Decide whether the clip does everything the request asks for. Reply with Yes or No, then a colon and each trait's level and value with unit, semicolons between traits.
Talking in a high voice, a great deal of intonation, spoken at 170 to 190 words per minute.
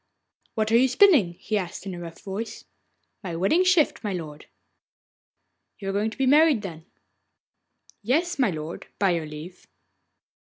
No: high, 200 Hz; wide, 7.1 semitones; average, 160 wpm